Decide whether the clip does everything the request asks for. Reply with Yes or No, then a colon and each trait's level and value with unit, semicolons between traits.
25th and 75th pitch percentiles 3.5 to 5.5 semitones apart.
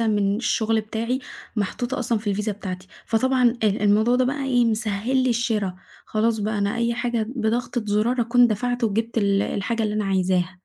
No: average, 2.8 semitones